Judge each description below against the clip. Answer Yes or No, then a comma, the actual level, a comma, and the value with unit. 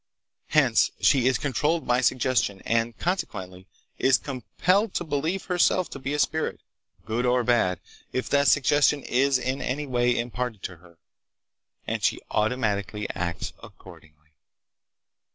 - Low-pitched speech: Yes, low, 125 Hz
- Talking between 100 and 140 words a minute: Yes, slow, 135 wpm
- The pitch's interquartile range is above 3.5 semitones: Yes, average, 5.2 semitones